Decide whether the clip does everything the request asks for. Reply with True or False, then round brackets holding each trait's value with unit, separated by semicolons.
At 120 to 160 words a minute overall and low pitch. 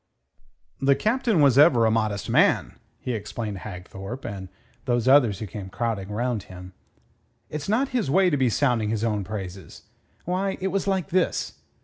False (170 wpm; 120 Hz)